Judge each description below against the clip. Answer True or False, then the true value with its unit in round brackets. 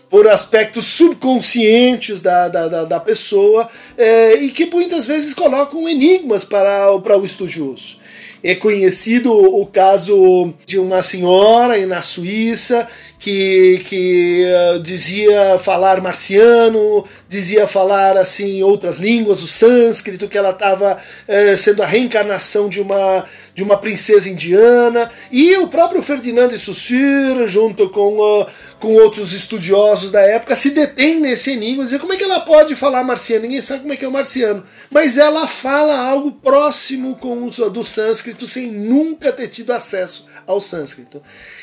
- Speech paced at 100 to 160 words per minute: True (155 wpm)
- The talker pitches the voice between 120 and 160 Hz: False (215 Hz)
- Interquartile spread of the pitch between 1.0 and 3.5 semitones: False (4.6 semitones)